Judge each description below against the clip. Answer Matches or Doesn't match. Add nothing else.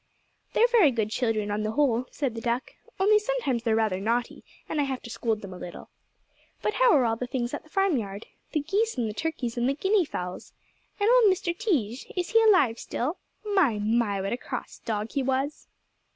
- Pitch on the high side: Matches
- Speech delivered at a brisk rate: Matches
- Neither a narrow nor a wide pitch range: Doesn't match